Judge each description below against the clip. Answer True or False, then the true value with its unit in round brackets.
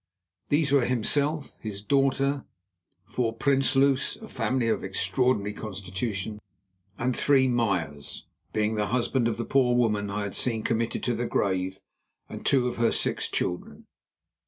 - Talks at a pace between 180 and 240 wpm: False (135 wpm)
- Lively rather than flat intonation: False (4.3 semitones)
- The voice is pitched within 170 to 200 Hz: False (115 Hz)